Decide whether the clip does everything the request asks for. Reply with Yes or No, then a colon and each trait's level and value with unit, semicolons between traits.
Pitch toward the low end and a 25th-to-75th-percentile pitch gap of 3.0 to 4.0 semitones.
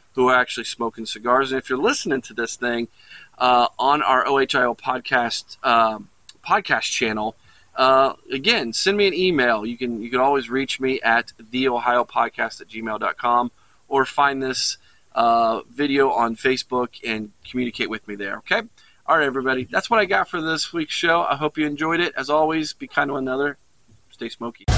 Yes: low, 125 Hz; average, 3.5 semitones